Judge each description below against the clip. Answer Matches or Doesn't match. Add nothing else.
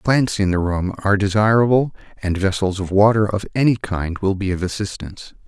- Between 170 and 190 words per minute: Matches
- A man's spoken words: Matches